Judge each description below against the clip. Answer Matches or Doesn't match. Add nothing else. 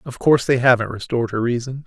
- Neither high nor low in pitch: Doesn't match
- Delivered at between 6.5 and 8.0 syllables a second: Matches